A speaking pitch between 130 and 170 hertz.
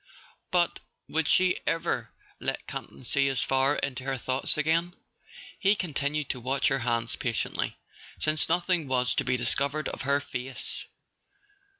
Yes: medium, 140 Hz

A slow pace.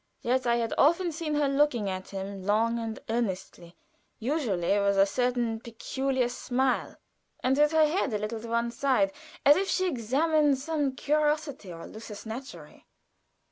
No: average, 160 wpm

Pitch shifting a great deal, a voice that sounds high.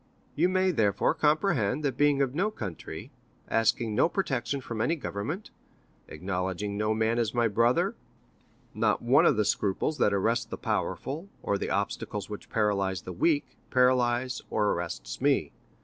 No: wide, 5.8 semitones; low, 115 Hz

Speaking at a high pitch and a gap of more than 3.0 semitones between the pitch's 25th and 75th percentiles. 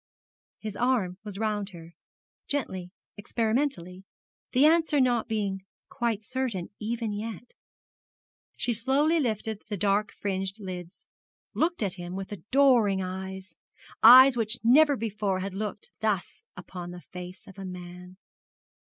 Yes: high, 210 Hz; average, 4.2 semitones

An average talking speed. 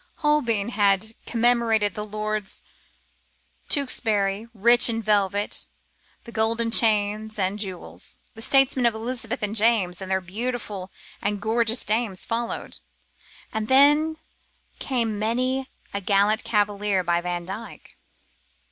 No: slow, 115 wpm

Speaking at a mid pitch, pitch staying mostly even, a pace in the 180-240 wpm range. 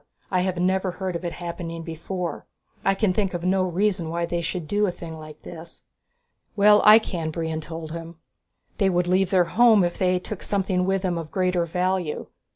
Yes: medium, 180 Hz; narrow, 2.2 semitones; average, 200 wpm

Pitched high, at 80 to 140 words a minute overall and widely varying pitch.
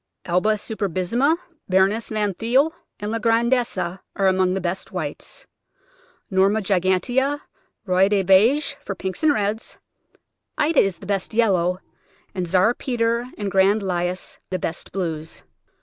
No: high, 195 Hz; slow, 135 wpm; average, 3.7 semitones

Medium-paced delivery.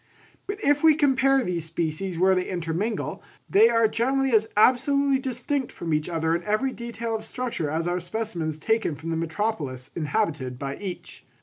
Yes: average, 175 wpm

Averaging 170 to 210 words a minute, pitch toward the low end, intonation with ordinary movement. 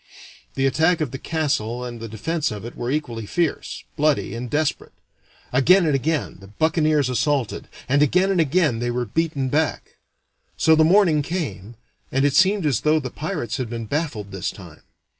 No: average, 180 wpm; medium, 145 Hz; average, 5.0 semitones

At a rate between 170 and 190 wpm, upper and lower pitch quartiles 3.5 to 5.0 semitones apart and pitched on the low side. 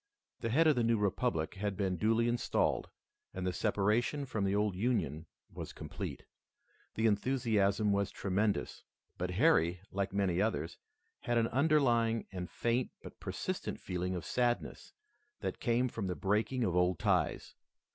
No: average, 155 wpm; average, 4.2 semitones; low, 105 Hz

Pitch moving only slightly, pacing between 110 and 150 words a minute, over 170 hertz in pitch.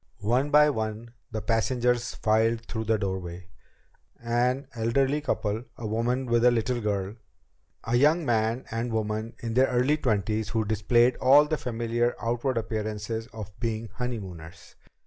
No: narrow, 2.2 semitones; average, 145 wpm; low, 115 Hz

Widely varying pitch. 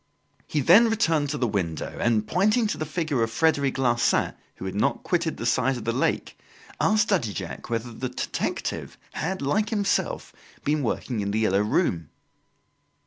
Yes: wide, 7.1 semitones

